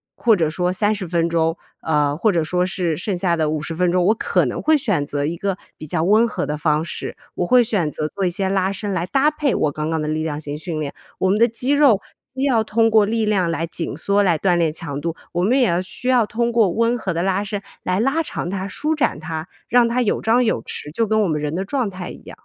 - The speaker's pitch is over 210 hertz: No, medium, 185 Hz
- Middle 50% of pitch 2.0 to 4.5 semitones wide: No, wide, 5.4 semitones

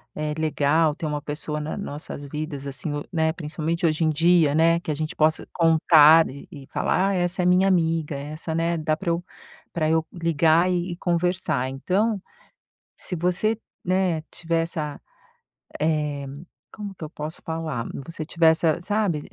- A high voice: No, medium, 160 Hz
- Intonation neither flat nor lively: No, narrow, 2.3 semitones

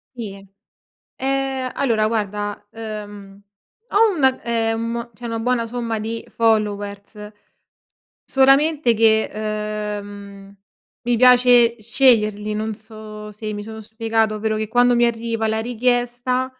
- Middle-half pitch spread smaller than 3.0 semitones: Yes, narrow, 2.4 semitones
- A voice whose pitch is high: Yes, high, 225 Hz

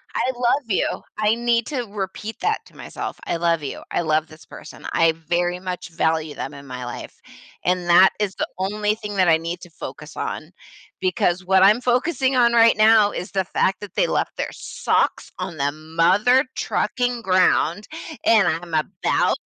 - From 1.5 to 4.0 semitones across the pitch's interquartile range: No, average, 4.9 semitones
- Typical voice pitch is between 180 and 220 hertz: Yes, medium, 185 Hz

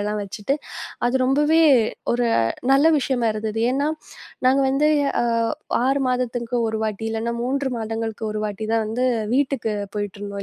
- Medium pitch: No, high, 235 Hz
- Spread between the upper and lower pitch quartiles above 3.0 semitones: Yes, average, 3.6 semitones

